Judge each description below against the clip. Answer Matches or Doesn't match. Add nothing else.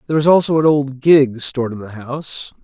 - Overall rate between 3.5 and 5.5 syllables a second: Doesn't match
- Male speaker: Matches